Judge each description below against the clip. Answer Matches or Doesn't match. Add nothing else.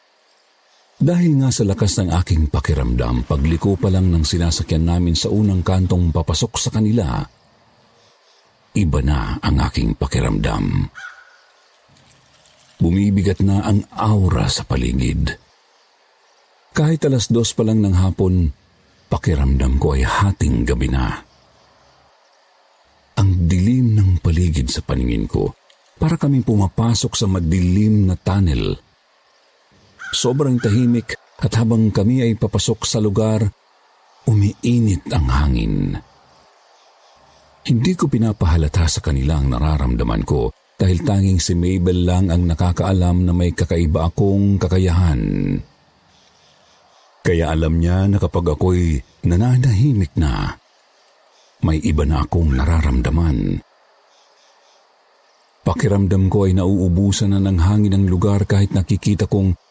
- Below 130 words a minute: Matches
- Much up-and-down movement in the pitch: Doesn't match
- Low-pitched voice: Matches